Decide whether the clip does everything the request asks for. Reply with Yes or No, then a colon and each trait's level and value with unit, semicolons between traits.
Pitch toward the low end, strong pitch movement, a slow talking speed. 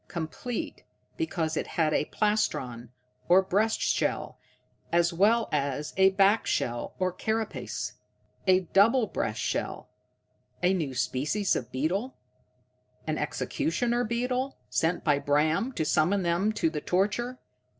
No: medium, 185 Hz; wide, 5.9 semitones; slow, 130 wpm